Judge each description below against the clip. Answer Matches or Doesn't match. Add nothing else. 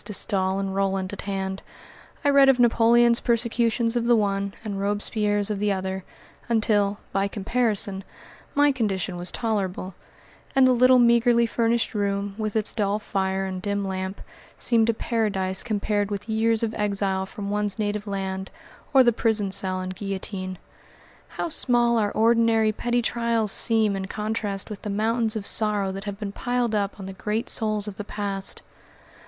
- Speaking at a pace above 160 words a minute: Matches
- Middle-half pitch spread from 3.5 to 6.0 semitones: Doesn't match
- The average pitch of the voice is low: Doesn't match